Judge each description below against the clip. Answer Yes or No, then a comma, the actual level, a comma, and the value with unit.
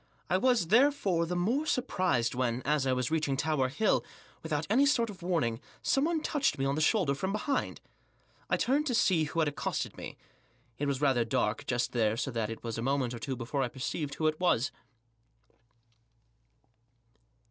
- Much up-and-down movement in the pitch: Yes, wide, 7.4 semitones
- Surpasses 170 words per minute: Yes, average, 185 wpm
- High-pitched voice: No, medium, 150 Hz